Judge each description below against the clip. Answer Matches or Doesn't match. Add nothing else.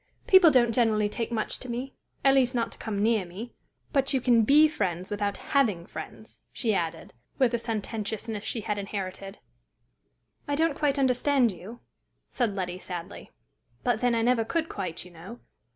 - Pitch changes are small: Doesn't match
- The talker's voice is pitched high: Matches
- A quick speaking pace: Doesn't match